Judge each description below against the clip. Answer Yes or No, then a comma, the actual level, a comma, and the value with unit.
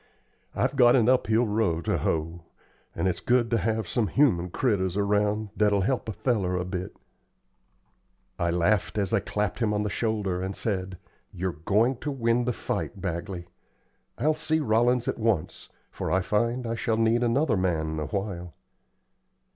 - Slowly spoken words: No, average, 165 wpm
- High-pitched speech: No, low, 105 Hz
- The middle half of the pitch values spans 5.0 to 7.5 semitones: No, average, 4.1 semitones